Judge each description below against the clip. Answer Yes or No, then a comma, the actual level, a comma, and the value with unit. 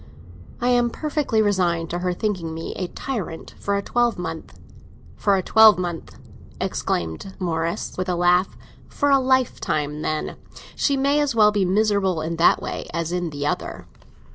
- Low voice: No, medium, 185 Hz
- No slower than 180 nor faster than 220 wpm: No, average, 160 wpm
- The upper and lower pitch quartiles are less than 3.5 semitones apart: No, average, 4.9 semitones